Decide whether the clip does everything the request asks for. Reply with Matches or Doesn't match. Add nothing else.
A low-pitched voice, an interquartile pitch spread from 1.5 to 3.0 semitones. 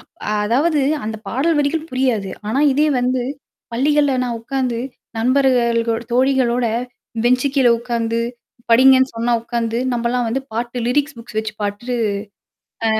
Doesn't match